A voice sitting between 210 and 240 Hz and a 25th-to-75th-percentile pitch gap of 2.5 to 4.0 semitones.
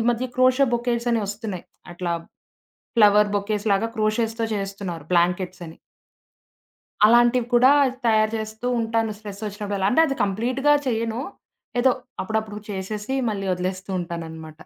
Yes: high, 215 Hz; average, 3.1 semitones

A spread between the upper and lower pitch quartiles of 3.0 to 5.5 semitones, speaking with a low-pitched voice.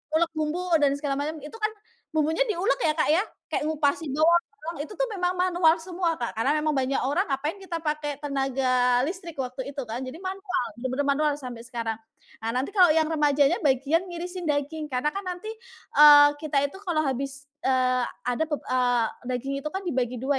No: average, 4.2 semitones; very high, 295 Hz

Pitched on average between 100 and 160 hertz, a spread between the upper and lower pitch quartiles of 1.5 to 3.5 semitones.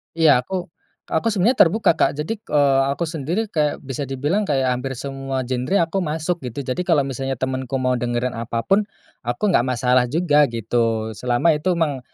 No: low, 135 Hz; average, 4.7 semitones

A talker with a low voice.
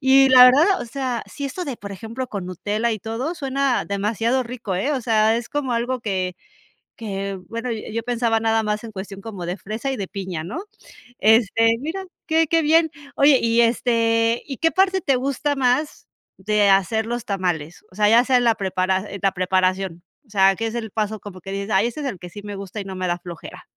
No: high, 225 Hz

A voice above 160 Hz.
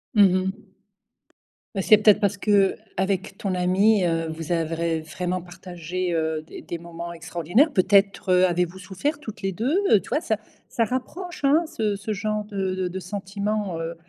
Yes: high, 190 Hz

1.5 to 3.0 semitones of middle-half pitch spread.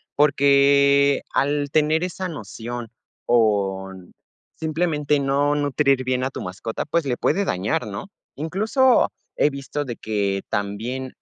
No: average, 4.9 semitones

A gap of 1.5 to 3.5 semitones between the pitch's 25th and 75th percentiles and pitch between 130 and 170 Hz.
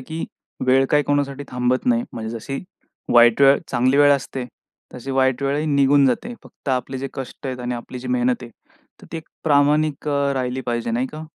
Yes: narrow, 2.4 semitones; low, 135 Hz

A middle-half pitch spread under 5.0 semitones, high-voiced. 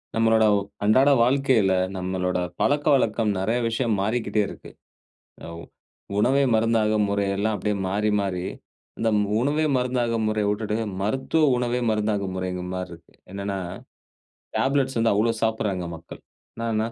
No: average, 3.3 semitones; low, 110 Hz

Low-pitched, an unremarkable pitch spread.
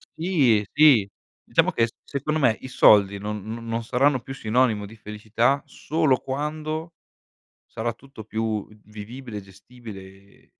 Yes: low, 115 Hz; average, 4.4 semitones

